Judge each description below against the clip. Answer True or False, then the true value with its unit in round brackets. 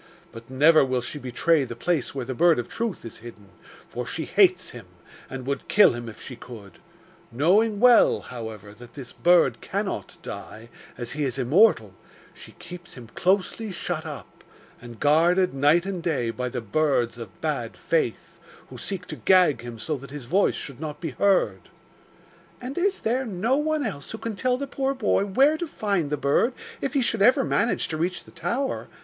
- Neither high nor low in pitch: True (155 Hz)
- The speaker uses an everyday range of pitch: False (8.5 semitones)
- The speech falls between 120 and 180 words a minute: False (190 wpm)